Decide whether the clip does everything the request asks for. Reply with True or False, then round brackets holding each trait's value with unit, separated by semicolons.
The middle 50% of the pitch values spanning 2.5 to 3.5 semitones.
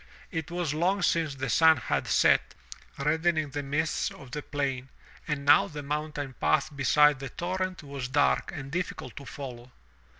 True (2.9 semitones)